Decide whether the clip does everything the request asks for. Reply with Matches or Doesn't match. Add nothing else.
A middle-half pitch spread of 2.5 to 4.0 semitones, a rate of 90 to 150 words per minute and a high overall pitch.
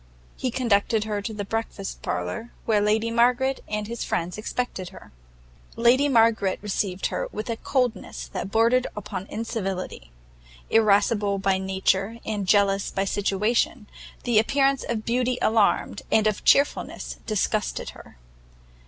Matches